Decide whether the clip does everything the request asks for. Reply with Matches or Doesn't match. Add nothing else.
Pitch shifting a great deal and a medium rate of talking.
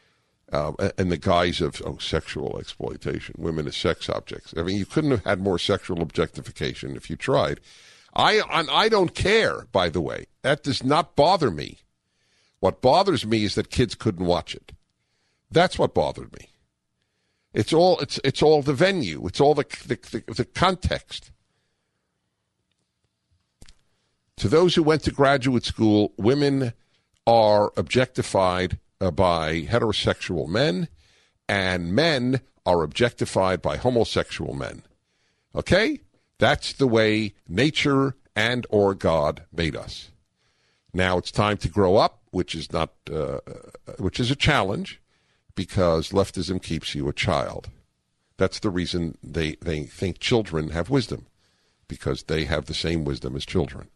Matches